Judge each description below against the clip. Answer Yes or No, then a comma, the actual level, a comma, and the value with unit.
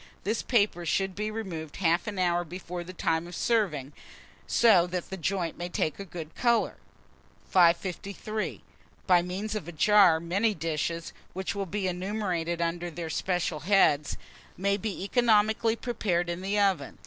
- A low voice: No, medium, 185 Hz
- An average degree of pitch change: Yes, average, 3.3 semitones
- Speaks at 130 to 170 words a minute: Yes, average, 160 wpm